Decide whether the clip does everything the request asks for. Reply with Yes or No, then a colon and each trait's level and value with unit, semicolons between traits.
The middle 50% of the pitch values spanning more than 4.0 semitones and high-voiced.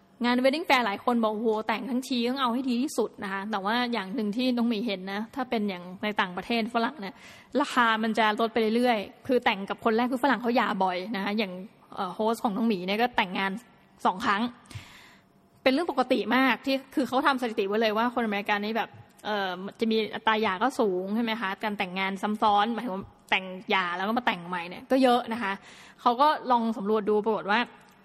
No: average, 3.1 semitones; high, 225 Hz